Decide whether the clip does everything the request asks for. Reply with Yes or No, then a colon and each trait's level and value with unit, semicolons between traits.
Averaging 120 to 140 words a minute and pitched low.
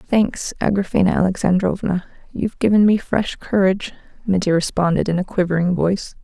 No: slow, 135 wpm; high, 190 Hz